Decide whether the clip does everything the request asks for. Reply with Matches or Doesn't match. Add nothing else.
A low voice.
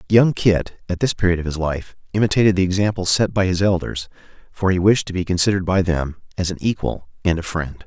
Matches